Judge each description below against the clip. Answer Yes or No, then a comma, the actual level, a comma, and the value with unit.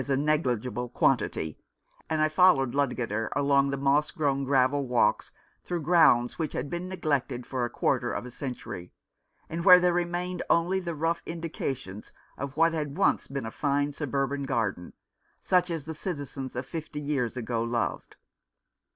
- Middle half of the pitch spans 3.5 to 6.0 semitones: Yes, average, 4.4 semitones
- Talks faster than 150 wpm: Yes, average, 165 wpm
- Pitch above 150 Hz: No, medium, 140 Hz